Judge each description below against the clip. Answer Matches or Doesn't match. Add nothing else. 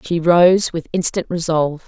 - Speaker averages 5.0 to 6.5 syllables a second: Doesn't match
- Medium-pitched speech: Matches